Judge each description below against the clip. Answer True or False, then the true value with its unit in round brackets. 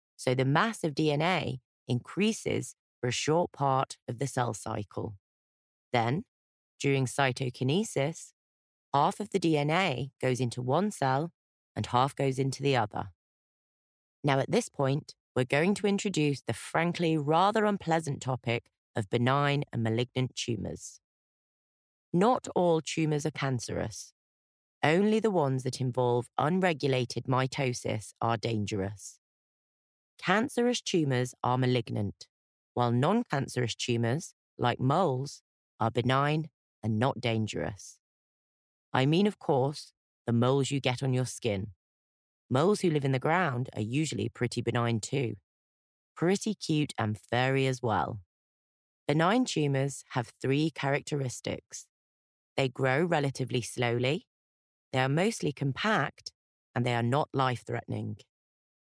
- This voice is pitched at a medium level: False (130 Hz)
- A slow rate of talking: True (125 wpm)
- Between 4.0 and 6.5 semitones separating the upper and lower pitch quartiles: True (4.7 semitones)